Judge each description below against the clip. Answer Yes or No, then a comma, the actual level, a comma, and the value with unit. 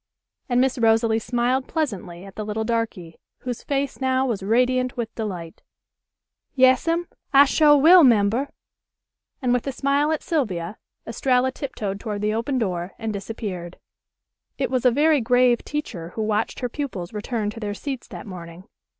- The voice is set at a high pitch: Yes, high, 235 Hz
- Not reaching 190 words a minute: Yes, average, 160 wpm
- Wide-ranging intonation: No, average, 4.1 semitones